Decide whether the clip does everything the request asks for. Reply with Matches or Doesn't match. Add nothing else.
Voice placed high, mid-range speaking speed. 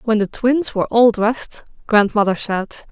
Matches